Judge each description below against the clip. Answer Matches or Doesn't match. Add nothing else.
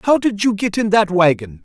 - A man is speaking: Matches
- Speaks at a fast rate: Matches